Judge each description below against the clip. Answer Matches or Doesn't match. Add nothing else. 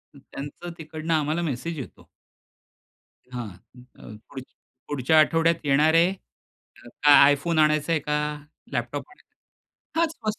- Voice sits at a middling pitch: Matches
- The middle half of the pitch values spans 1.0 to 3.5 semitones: Matches